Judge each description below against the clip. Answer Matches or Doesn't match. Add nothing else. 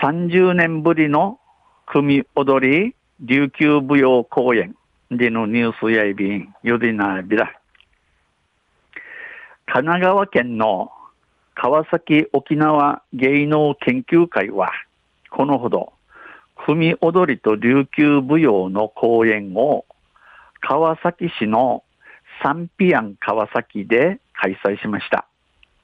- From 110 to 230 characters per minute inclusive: Matches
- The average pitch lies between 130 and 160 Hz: Matches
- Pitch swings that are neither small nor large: Doesn't match